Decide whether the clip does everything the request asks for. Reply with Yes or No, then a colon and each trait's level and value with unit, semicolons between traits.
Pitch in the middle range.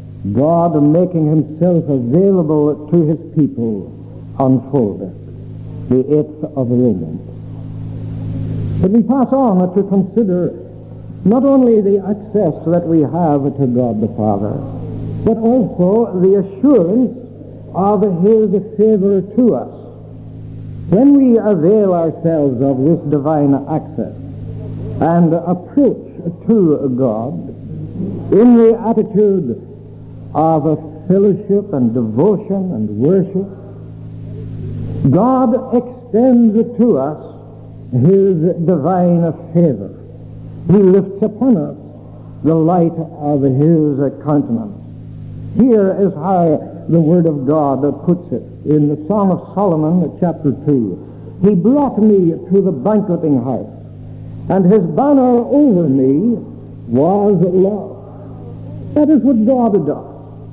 Yes: medium, 160 Hz